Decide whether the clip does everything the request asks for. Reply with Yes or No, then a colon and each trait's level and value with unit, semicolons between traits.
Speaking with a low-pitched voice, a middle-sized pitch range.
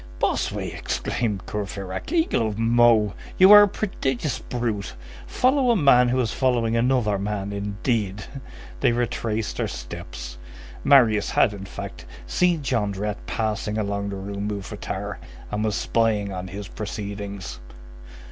Yes: low, 105 Hz; average, 3.3 semitones